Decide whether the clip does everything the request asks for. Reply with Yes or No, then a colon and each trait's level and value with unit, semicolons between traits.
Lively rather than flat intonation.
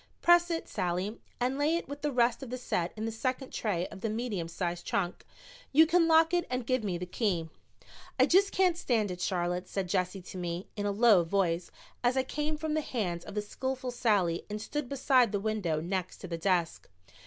Yes: wide, 6.7 semitones